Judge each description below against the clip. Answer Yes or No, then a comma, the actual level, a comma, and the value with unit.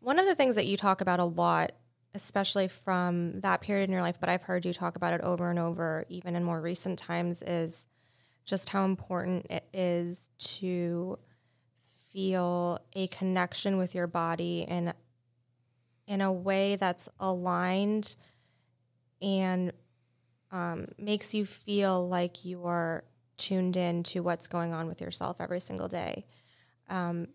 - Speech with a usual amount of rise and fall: No, narrow, 2.0 semitones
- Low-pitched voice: No, medium, 180 Hz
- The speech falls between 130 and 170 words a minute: Yes, average, 155 wpm